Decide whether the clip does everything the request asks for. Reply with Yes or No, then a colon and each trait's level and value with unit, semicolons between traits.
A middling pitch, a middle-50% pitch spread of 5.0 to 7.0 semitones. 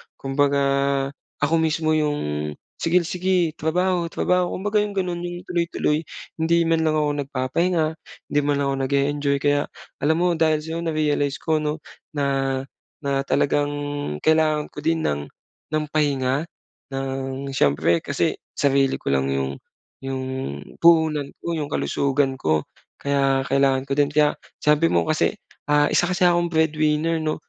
No: medium, 150 Hz; average, 3.1 semitones